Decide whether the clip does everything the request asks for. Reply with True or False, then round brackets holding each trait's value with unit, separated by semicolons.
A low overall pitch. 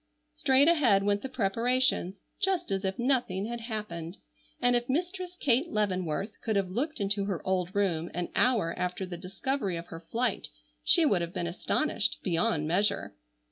False (205 Hz)